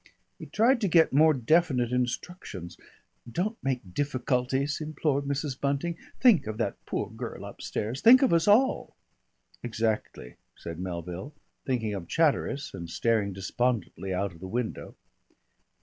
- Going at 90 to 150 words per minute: Yes, slow, 135 wpm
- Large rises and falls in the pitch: Yes, wide, 7.0 semitones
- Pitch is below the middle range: Yes, low, 130 Hz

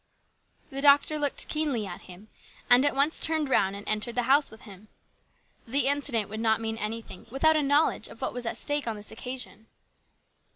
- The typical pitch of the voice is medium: No, high, 245 Hz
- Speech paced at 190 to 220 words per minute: Yes, average, 200 wpm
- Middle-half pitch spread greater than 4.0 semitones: Yes, average, 4.7 semitones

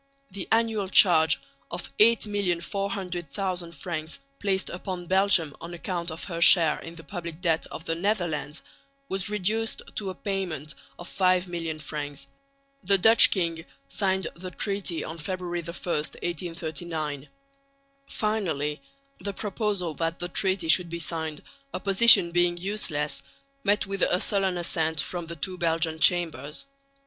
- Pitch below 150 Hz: No, medium, 175 Hz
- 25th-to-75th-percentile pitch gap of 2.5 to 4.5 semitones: Yes, average, 3.0 semitones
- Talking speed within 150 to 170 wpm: No, slow, 135 wpm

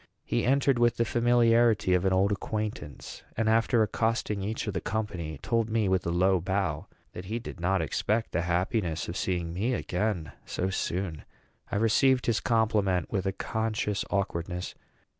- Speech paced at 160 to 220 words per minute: Yes, average, 170 wpm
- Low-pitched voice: Yes, low, 100 Hz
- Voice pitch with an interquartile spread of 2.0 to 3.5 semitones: No, average, 3.9 semitones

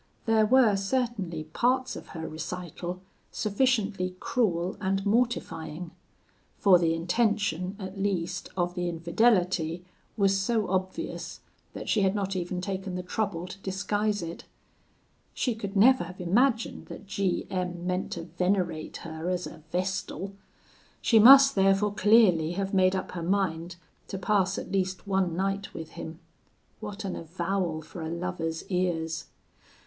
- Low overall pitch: No, medium, 185 Hz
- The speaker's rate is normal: Yes, average, 145 wpm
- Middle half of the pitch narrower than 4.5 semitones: Yes, average, 2.7 semitones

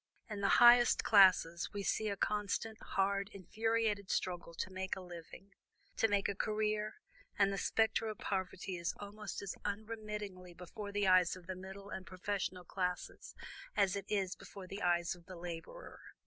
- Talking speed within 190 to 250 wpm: No, average, 170 wpm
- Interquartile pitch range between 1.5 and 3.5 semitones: Yes, narrow, 2.4 semitones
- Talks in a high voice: Yes, high, 195 Hz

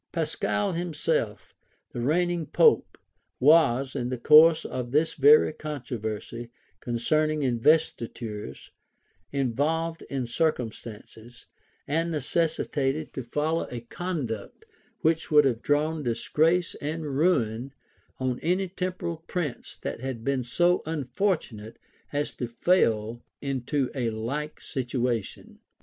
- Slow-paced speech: Yes, slow, 110 wpm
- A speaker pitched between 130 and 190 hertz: Yes, medium, 140 Hz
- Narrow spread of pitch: No, average, 5.1 semitones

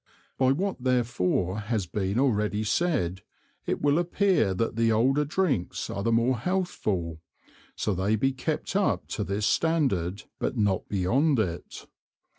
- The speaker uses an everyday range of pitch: No, wide, 6.5 semitones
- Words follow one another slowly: No, average, 145 wpm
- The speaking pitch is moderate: No, low, 115 Hz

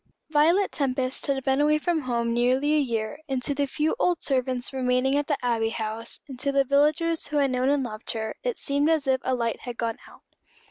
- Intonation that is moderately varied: Yes, average, 3.1 semitones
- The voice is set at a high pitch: Yes, very high, 270 Hz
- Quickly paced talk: Yes, fast, 225 wpm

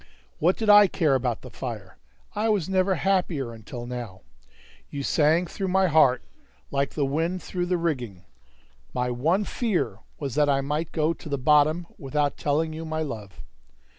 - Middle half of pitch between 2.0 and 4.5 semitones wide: No, average, 5.2 semitones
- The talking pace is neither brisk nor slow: Yes, average, 170 wpm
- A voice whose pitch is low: No, medium, 150 Hz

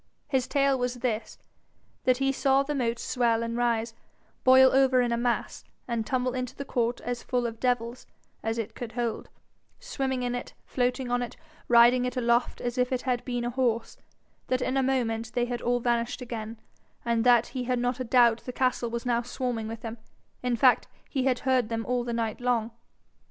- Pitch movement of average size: No, narrow, 1.4 semitones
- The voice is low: No, high, 245 Hz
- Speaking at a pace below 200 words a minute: No, fast, 205 wpm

